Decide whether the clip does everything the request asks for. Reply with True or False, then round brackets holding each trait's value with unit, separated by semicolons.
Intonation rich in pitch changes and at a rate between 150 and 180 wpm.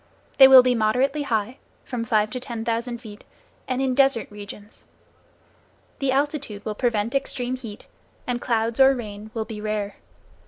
False (3.3 semitones; 160 wpm)